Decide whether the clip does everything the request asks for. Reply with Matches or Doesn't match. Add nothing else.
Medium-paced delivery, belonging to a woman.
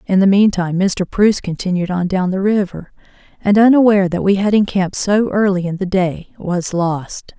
Matches